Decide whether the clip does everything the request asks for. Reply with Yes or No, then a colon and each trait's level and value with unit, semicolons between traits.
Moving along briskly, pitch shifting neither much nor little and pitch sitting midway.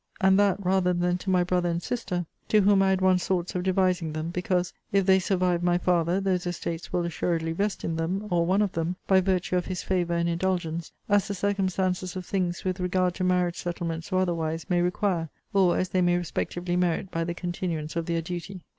No: fast, 215 wpm; narrow, 1.6 semitones; medium, 180 Hz